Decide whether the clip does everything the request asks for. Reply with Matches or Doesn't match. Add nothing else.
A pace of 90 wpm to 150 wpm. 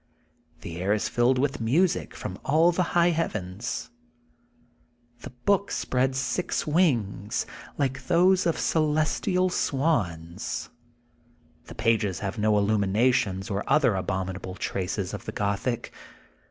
Matches